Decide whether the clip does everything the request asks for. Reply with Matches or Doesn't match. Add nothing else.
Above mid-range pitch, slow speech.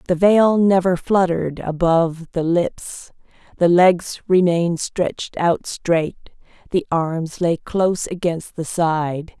Doesn't match